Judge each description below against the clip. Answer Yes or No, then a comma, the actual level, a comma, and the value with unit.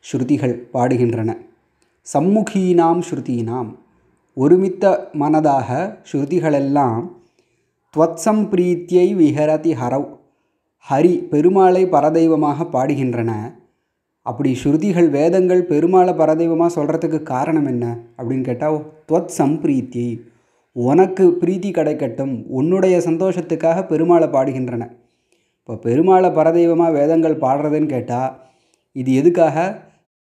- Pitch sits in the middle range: Yes, medium, 155 Hz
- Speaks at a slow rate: No, average, 85 wpm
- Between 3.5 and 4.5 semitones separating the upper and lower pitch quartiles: No, average, 5.0 semitones